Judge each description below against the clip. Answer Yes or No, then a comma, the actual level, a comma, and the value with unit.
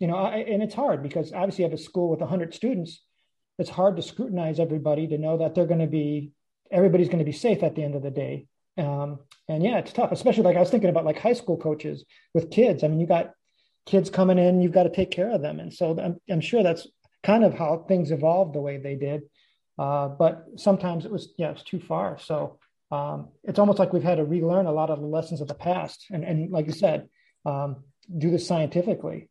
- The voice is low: No, medium, 170 Hz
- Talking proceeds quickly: Yes, fast, 245 wpm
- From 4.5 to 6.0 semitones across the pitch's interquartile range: No, average, 3.4 semitones